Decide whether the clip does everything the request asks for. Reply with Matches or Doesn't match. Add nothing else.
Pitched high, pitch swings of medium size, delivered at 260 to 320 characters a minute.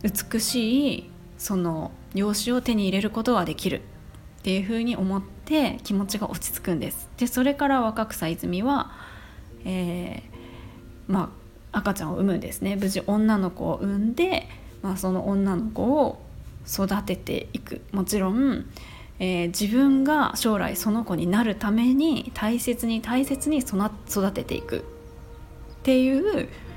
Matches